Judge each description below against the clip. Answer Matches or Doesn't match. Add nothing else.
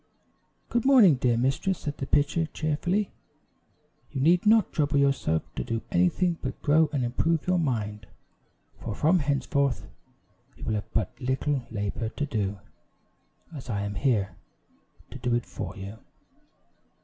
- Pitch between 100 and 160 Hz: Matches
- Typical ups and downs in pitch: Doesn't match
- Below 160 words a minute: Matches